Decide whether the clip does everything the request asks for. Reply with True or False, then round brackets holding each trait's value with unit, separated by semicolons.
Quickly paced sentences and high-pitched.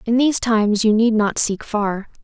True (215 wpm; 220 Hz)